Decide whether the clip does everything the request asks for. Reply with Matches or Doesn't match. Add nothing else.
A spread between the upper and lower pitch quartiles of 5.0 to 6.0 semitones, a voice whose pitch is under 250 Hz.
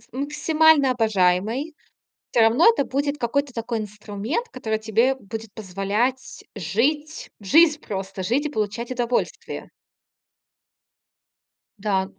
Matches